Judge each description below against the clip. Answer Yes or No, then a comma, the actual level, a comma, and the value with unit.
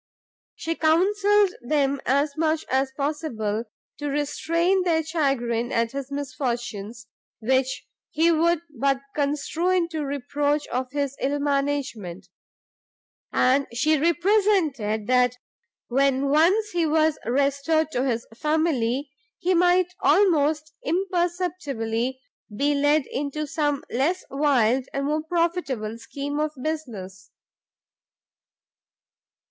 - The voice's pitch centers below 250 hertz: No, very high, 285 Hz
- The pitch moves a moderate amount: Yes, average, 3.7 semitones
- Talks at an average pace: No, slow, 110 wpm